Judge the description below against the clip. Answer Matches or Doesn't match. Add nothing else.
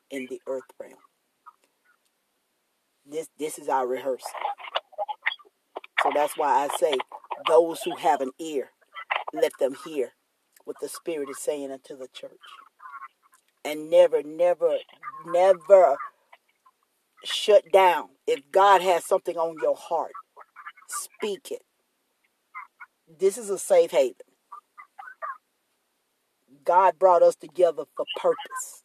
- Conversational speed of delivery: Doesn't match